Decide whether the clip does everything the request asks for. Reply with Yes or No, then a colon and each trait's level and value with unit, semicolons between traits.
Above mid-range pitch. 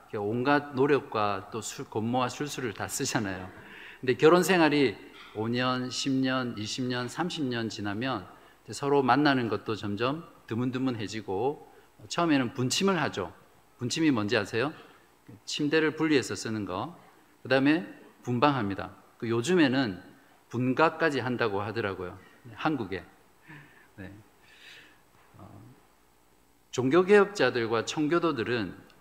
No: low, 125 Hz